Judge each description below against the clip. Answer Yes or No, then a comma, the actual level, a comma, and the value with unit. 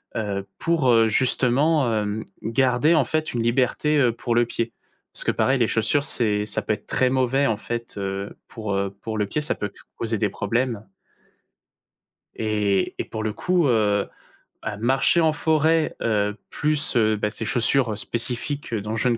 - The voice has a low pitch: Yes, low, 115 Hz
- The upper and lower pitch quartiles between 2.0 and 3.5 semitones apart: No, average, 4.1 semitones